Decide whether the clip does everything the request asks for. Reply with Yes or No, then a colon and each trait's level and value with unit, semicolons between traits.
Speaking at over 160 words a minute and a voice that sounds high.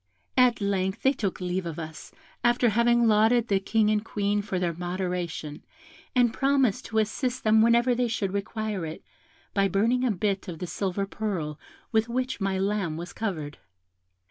Yes: average, 170 wpm; high, 205 Hz